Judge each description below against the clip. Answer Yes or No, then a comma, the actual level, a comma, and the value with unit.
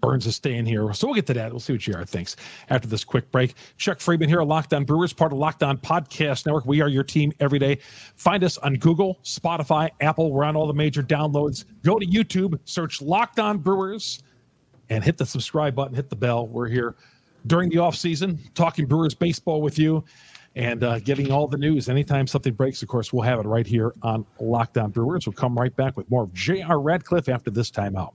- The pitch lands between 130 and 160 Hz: Yes, medium, 140 Hz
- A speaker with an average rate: No, fast, 220 wpm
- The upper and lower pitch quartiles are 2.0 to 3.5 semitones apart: No, average, 4.7 semitones